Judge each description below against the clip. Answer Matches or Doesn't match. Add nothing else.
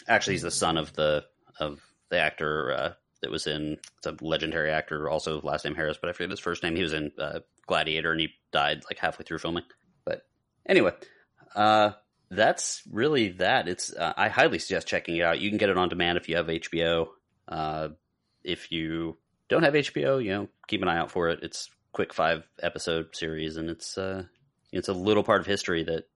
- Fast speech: Matches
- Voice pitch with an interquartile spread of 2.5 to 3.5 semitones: Matches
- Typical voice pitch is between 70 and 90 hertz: Matches